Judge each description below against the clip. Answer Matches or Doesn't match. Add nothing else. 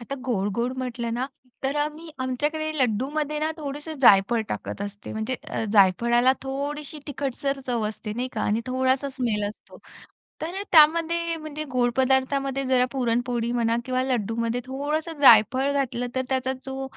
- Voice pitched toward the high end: Matches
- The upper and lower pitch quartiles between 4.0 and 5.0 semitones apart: Doesn't match